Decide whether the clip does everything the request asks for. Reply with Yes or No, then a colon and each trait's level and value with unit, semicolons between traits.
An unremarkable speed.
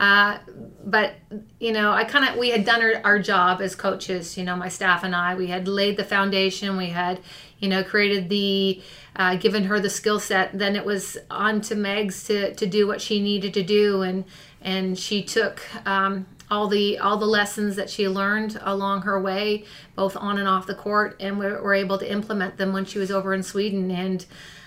No: fast, 215 wpm